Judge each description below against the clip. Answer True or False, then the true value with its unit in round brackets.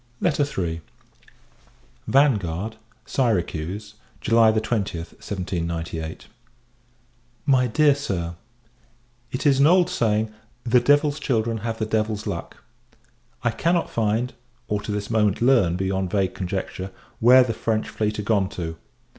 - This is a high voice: False (110 Hz)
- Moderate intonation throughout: True (4.6 semitones)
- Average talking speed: False (120 wpm)